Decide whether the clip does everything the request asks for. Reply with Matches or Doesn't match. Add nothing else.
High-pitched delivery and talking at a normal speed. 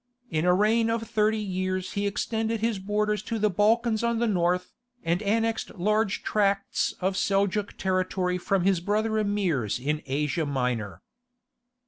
Matches